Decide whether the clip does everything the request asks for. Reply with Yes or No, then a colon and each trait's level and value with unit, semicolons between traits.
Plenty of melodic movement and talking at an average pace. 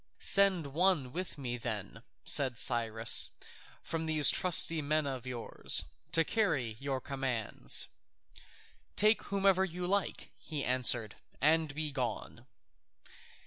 No: wide, 5.8 semitones; slow, 115 wpm